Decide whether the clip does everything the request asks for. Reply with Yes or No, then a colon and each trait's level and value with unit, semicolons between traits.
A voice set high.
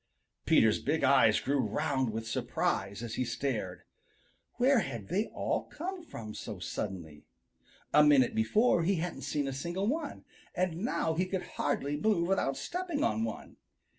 No: medium, 145 Hz